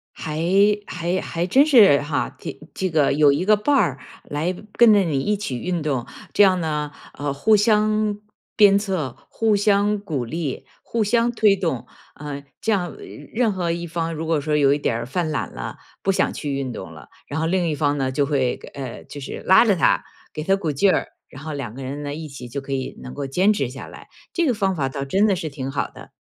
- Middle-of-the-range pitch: Yes, medium, 160 Hz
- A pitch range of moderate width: No, wide, 6.1 semitones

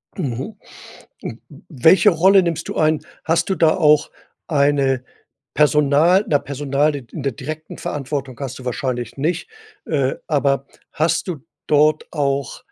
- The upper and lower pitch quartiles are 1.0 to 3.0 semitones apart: Yes, average, 2.7 semitones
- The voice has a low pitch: No, medium, 145 Hz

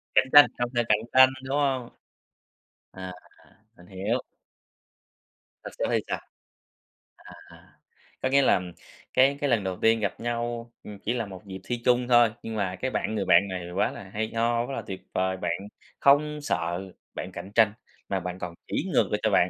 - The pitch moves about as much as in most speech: Yes, average, 4.8 semitones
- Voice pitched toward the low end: Yes, low, 115 Hz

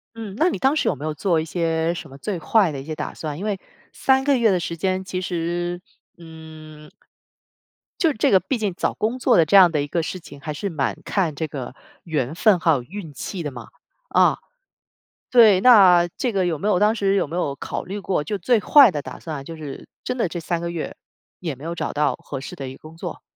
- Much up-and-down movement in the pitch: No, average, 4.4 semitones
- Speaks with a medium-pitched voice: Yes, medium, 170 Hz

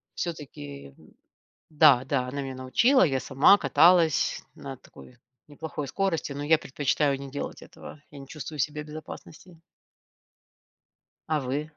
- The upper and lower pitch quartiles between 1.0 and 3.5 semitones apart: Yes, average, 2.8 semitones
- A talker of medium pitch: Yes, medium, 145 Hz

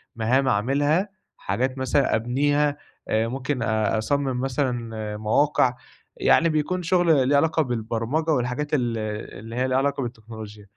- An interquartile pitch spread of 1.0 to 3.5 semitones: No, average, 4.1 semitones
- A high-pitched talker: No, low, 130 Hz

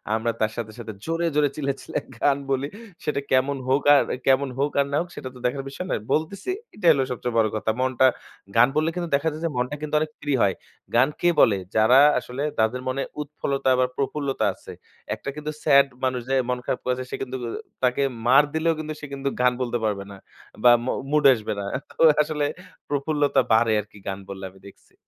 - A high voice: No, low, 135 Hz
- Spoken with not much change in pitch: No, average, 3.2 semitones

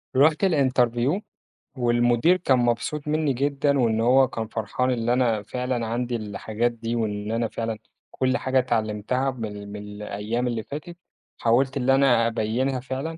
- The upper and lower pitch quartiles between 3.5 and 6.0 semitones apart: No, average, 2.8 semitones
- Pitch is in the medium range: No, low, 120 Hz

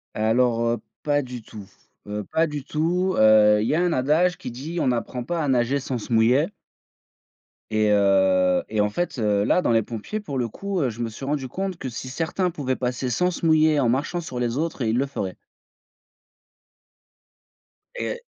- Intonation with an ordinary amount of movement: No, wide, 6.0 semitones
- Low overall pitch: Yes, low, 130 Hz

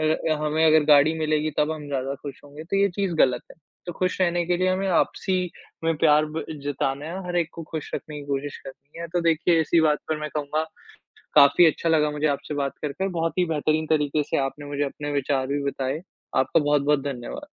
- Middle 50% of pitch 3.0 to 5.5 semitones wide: No, narrow, 2.4 semitones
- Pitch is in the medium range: Yes, medium, 150 Hz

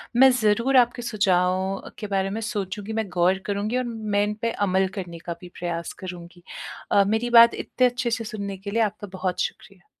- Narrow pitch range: No, average, 3.2 semitones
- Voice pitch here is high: Yes, high, 205 Hz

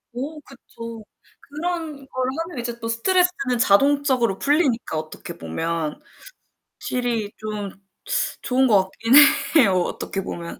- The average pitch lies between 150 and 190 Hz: No, high, 240 Hz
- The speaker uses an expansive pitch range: Yes, wide, 5.8 semitones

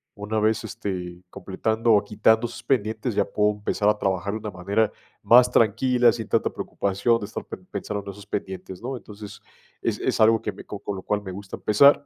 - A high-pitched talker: No, low, 105 Hz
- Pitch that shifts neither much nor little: No, narrow, 2.0 semitones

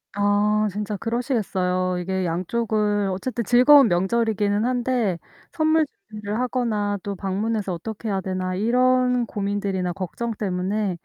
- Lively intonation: No, average, 3.7 semitones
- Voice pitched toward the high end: Yes, high, 210 Hz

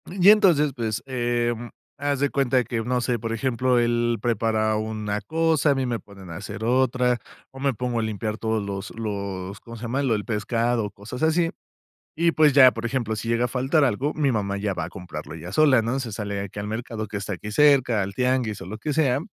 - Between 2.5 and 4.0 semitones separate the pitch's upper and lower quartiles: Yes, average, 3.6 semitones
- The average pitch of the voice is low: Yes, low, 120 Hz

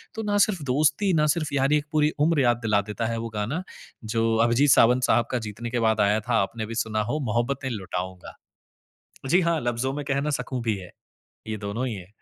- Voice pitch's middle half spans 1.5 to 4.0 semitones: No, average, 5.0 semitones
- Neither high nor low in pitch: No, low, 120 Hz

